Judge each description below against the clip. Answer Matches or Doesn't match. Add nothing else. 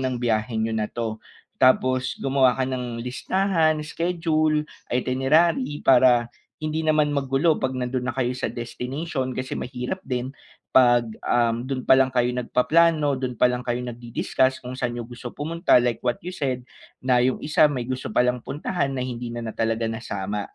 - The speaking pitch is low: Matches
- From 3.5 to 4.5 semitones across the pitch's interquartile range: Doesn't match